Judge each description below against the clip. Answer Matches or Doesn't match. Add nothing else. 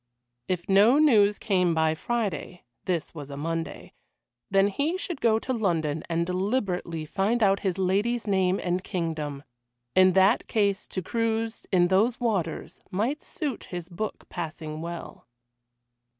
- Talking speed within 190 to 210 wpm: Doesn't match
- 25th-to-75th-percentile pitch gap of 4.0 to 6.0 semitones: Matches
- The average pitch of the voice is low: Doesn't match